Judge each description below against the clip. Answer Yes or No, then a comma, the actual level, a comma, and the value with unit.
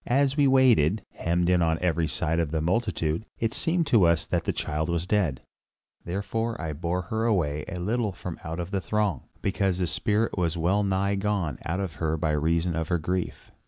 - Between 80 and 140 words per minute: No, average, 200 wpm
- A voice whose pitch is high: No, very low, 90 Hz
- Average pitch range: Yes, average, 4.3 semitones